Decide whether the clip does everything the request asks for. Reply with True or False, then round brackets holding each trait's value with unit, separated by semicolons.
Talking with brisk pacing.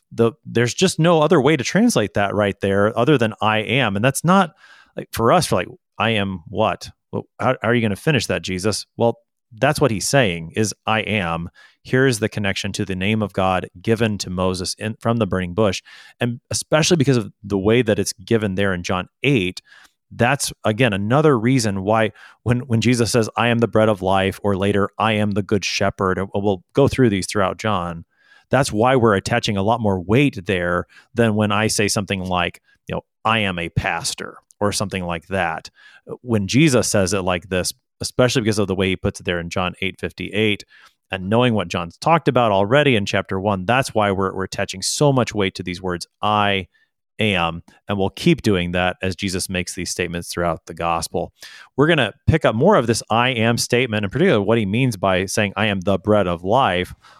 True (215 wpm)